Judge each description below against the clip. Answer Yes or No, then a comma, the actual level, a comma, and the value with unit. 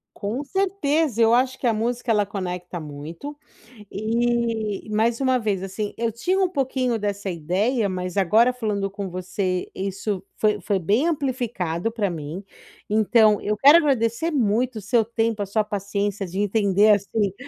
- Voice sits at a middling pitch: No, high, 215 Hz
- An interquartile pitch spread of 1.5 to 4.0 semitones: Yes, average, 3.5 semitones